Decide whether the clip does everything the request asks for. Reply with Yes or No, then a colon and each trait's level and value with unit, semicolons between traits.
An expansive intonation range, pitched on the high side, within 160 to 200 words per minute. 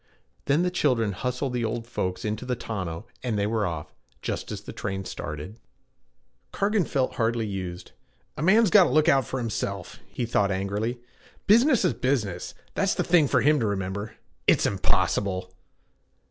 No: wide, 5.9 semitones; low, 115 Hz; average, 170 wpm